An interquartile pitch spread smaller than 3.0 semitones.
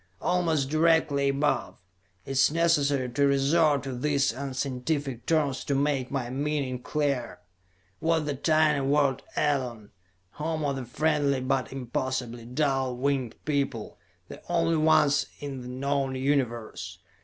Yes: narrow, 2.5 semitones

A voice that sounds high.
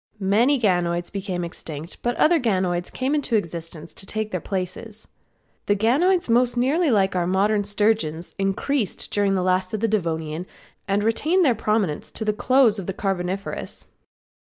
Yes: high, 205 Hz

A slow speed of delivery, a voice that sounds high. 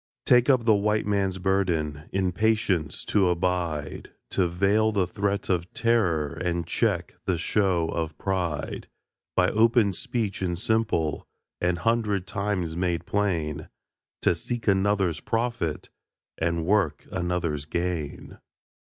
No: slow, 125 wpm; very low, 90 Hz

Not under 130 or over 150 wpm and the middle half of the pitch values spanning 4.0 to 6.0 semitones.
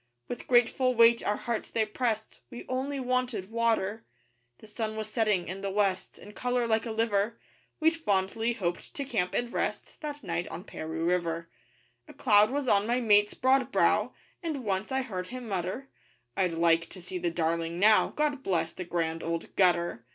No: average, 185 wpm; average, 5.3 semitones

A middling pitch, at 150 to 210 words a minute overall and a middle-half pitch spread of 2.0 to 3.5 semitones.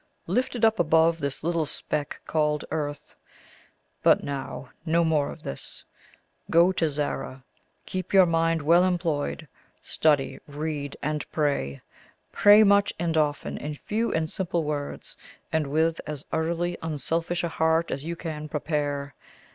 No: medium, 160 Hz; average, 140 wpm; narrow, 2.5 semitones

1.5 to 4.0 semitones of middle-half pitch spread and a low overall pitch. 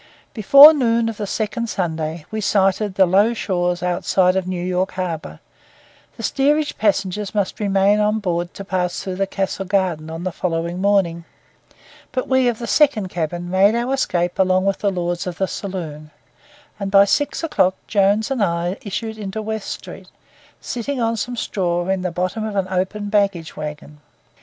No: average, 3.4 semitones; high, 195 Hz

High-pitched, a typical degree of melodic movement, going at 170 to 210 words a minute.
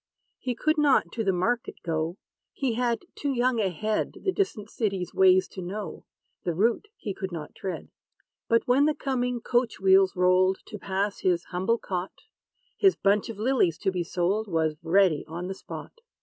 Yes: high, 195 Hz; average, 4.9 semitones; average, 180 wpm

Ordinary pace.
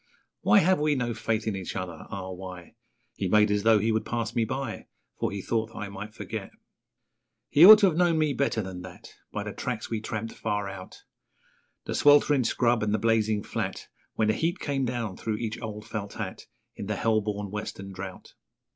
No: fast, 210 wpm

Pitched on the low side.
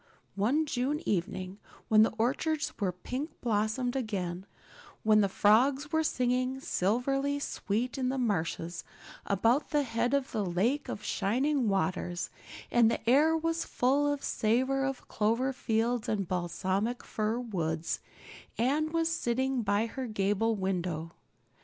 No: high, 230 Hz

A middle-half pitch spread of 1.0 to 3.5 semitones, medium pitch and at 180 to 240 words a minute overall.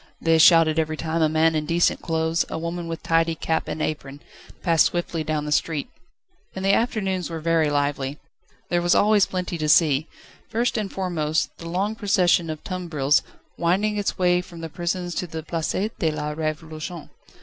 Yes: narrow, 2.4 semitones; medium, 165 Hz; average, 185 wpm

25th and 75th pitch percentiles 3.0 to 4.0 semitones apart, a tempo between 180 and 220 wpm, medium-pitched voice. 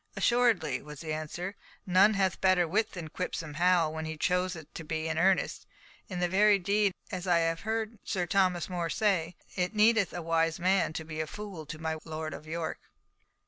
Yes: average, 3.3 semitones; average, 185 wpm; medium, 175 Hz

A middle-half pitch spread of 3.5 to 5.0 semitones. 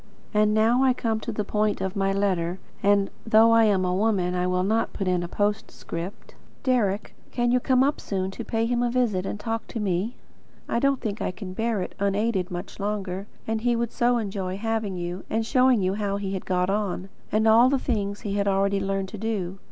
No: average, 2.9 semitones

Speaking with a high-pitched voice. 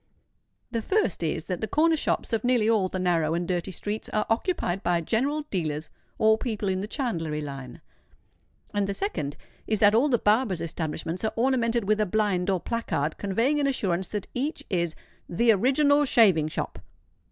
Yes: high, 210 Hz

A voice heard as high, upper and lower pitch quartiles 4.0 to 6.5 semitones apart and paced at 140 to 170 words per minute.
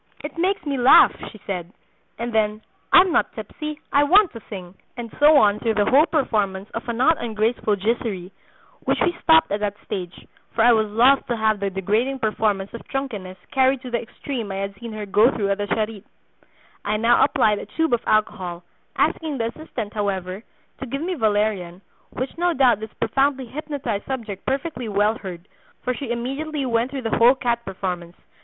No: high, 230 Hz; average, 4.7 semitones; average, 190 wpm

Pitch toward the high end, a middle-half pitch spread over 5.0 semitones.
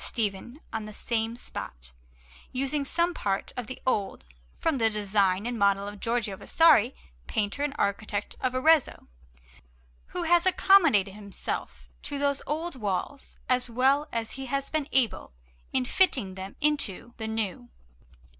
Yes: high, 235 Hz; wide, 5.6 semitones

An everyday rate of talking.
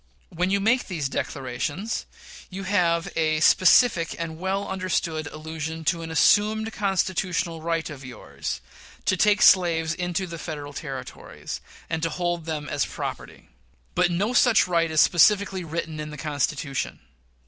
Yes: average, 150 wpm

